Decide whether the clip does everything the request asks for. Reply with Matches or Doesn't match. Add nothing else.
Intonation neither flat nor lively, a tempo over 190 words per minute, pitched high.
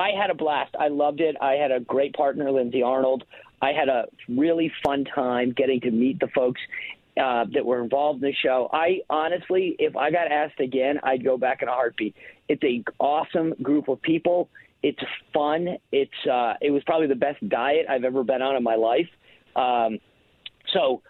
Doesn't match